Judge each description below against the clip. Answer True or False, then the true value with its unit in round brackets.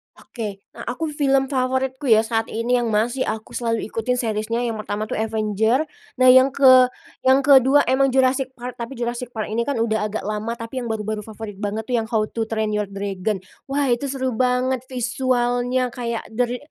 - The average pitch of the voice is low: False (240 Hz)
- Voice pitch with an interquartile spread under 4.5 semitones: True (2.9 semitones)